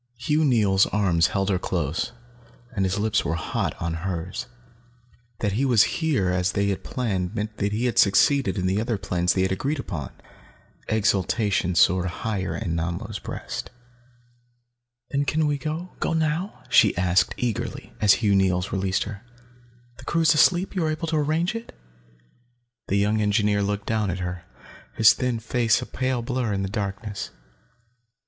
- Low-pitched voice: Yes, low, 105 Hz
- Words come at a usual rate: Yes, average, 170 wpm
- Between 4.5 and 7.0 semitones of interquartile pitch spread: Yes, average, 5.2 semitones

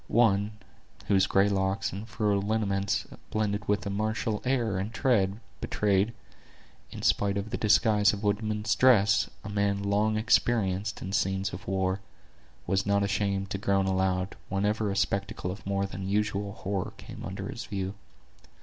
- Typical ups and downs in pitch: No, narrow, 1.5 semitones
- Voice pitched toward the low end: Yes, low, 100 Hz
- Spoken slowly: No, average, 160 wpm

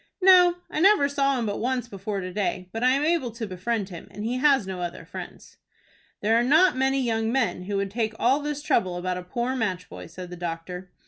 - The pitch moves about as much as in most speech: No, wide, 6.3 semitones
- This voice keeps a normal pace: No, fast, 235 wpm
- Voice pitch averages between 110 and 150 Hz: No, high, 225 Hz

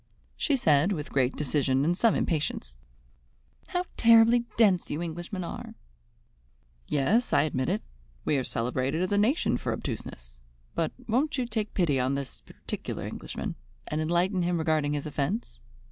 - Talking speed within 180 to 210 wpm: No, average, 155 wpm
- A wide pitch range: Yes, wide, 7.1 semitones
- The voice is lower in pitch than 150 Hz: No, medium, 160 Hz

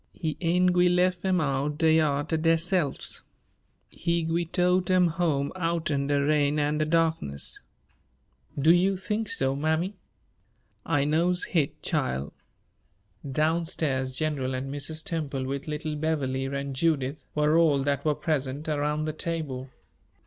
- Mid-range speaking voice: Yes, medium, 155 Hz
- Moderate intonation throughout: Yes, average, 3.1 semitones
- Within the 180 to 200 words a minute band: No, average, 140 wpm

